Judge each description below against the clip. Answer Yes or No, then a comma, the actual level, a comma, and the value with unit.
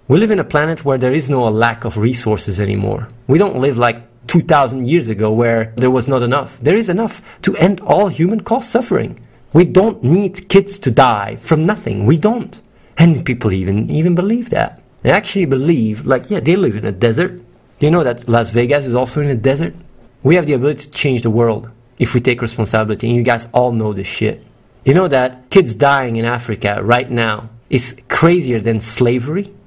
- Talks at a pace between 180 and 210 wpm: Yes, fast, 205 wpm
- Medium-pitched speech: No, low, 130 Hz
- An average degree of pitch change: No, wide, 6.4 semitones